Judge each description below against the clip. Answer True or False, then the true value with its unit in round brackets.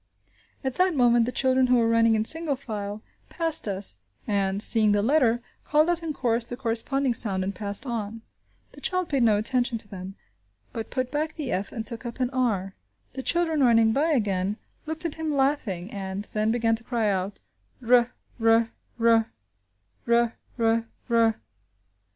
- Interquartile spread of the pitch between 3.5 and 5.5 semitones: True (4.3 semitones)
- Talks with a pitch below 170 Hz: False (230 Hz)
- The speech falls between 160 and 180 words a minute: True (170 wpm)